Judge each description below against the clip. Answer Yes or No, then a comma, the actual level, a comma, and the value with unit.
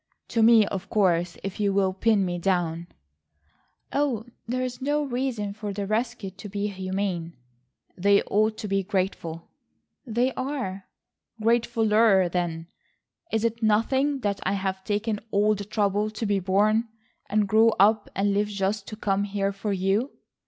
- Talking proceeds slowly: No, average, 160 wpm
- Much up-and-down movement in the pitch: No, narrow, 2.5 semitones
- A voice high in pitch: Yes, high, 205 Hz